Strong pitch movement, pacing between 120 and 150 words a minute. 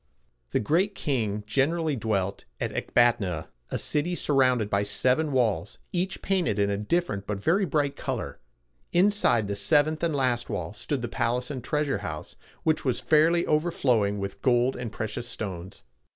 No: wide, 6.7 semitones; average, 165 wpm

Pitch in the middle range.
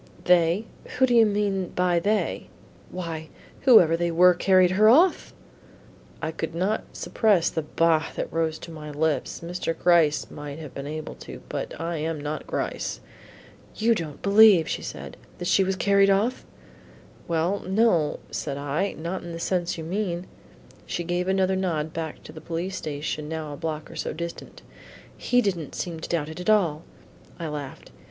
Yes: medium, 170 Hz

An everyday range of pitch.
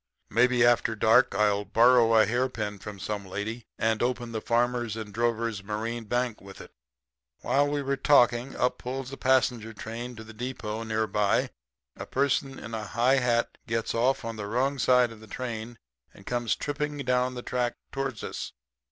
No: narrow, 2.3 semitones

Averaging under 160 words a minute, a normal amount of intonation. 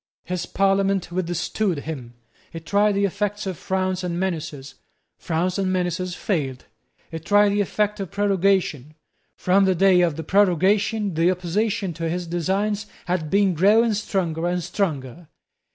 Yes: average, 150 wpm; average, 3.0 semitones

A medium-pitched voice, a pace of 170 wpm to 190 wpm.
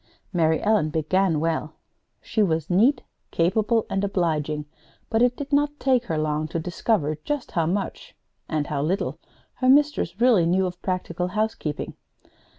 No: medium, 180 Hz; average, 155 wpm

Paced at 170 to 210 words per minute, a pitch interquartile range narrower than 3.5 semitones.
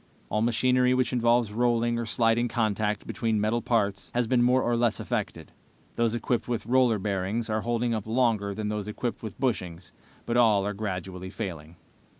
Yes: average, 175 wpm; narrow, 2.5 semitones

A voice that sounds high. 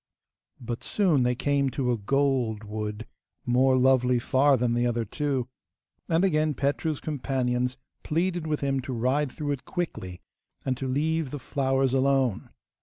No: low, 135 Hz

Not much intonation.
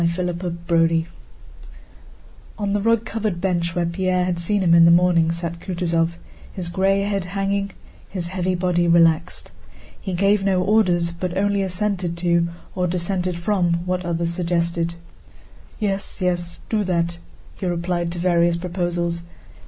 Yes: narrow, 1.9 semitones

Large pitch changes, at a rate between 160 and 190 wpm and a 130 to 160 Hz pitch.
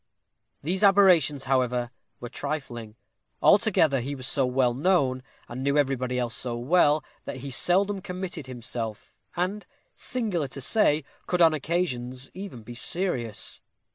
No: wide, 6.1 semitones; average, 140 wpm; medium, 140 Hz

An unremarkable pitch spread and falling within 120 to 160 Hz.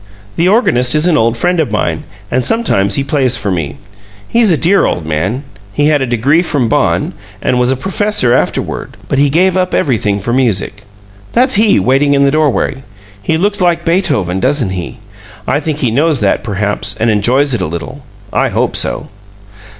No: wide, 7.4 semitones; low, 135 Hz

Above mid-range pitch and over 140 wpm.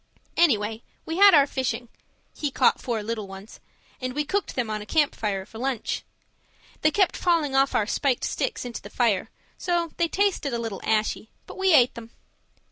Yes: very high, 255 Hz; average, 190 wpm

